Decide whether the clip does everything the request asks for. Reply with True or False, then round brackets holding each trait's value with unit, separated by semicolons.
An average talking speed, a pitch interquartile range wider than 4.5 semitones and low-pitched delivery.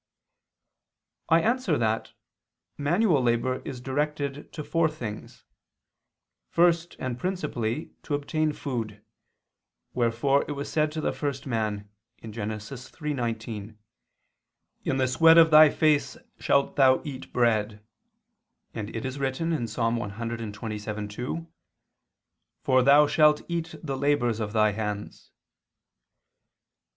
False (115 wpm; 5.1 semitones; 130 Hz)